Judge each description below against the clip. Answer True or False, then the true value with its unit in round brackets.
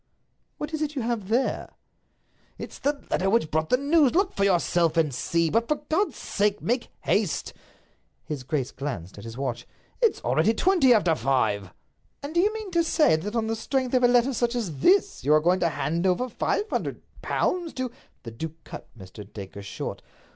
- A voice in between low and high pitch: False (210 Hz)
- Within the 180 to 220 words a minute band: True (195 wpm)